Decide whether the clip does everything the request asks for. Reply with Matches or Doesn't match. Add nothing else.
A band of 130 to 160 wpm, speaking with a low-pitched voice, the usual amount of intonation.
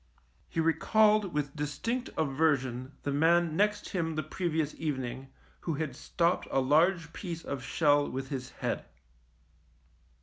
Doesn't match